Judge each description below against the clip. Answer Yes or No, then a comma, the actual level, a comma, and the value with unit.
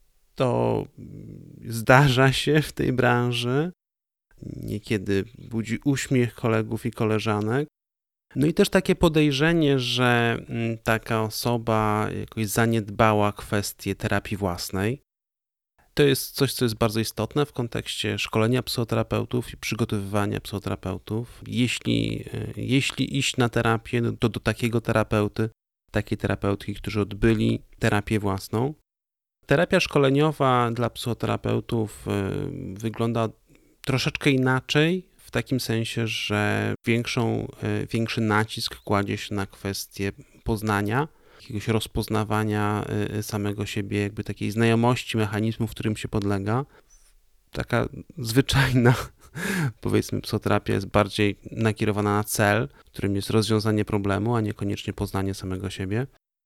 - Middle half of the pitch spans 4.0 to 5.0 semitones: No, average, 3.3 semitones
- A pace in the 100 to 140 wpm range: Yes, slow, 110 wpm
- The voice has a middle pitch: No, low, 115 Hz